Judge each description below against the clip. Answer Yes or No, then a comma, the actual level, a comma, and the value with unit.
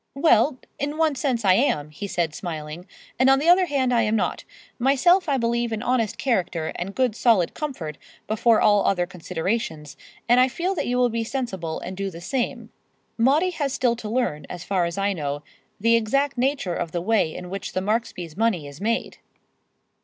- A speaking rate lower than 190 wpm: No, average, 200 wpm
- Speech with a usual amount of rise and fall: No, wide, 6.5 semitones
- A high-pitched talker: Yes, high, 225 Hz